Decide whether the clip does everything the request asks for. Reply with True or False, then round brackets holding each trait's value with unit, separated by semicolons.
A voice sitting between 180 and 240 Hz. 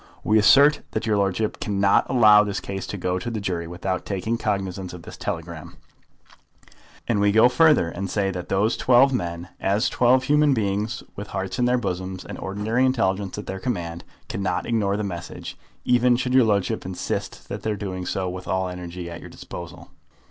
False (100 Hz)